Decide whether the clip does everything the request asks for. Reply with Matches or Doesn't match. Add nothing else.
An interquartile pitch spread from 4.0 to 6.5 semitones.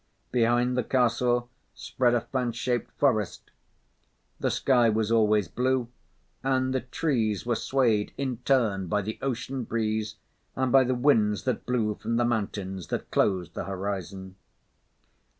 Doesn't match